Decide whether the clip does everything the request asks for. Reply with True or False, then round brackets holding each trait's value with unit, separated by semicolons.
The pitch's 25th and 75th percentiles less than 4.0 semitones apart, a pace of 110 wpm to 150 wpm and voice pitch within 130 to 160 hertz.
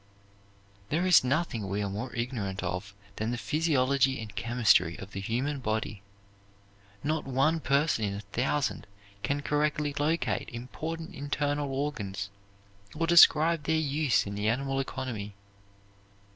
False (5.6 semitones; 135 wpm; 135 Hz)